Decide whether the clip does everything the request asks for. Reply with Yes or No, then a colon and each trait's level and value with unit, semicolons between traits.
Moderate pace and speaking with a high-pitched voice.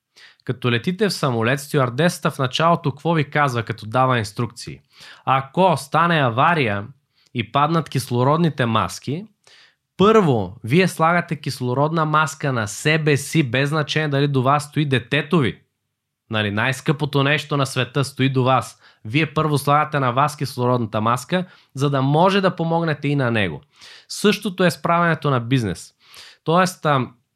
No: average, 145 wpm; medium, 140 Hz